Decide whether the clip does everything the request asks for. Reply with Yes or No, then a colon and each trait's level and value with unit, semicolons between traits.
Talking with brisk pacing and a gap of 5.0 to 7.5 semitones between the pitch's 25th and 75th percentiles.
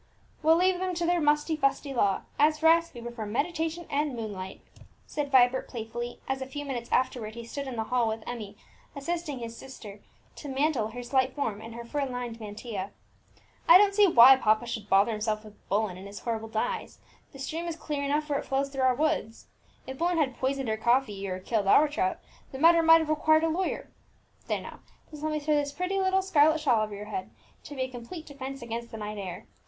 Yes: fast, 220 wpm; average, 5.3 semitones